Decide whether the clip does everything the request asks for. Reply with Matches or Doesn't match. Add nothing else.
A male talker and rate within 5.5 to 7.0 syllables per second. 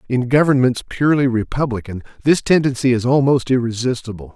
Matches